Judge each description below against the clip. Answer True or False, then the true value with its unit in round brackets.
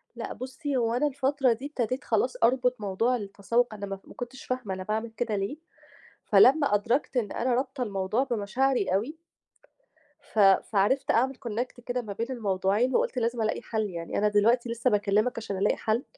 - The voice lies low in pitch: False (230 Hz)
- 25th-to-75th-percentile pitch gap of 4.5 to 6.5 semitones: False (3.7 semitones)